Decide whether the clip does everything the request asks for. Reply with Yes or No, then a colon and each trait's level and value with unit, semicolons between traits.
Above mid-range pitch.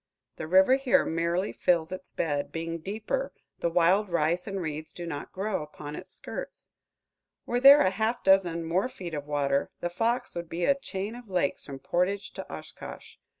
No: medium, 180 Hz